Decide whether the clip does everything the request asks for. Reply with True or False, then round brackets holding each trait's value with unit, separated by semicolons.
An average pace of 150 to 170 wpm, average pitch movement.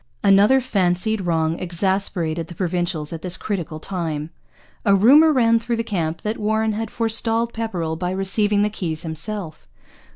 True (155 wpm; 4.8 semitones)